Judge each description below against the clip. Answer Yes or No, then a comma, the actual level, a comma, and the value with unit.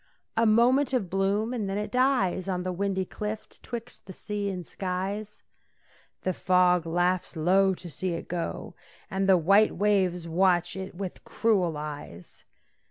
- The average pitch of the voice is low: No, high, 190 Hz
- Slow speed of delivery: No, average, 160 wpm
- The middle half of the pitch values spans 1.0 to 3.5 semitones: Yes, average, 2.8 semitones